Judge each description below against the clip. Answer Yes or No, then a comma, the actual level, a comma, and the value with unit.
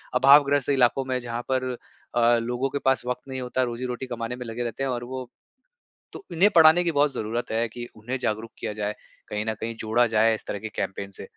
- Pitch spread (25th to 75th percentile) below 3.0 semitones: Yes, narrow, 2.6 semitones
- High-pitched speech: No, low, 120 Hz